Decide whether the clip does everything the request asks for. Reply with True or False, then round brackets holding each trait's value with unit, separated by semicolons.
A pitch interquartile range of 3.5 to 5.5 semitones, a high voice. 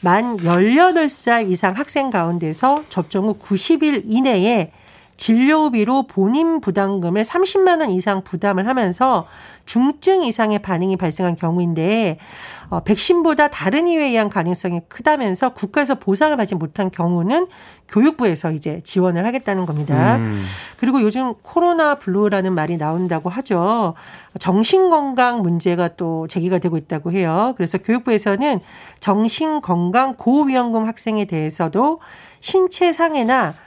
False (6.9 semitones; 210 Hz)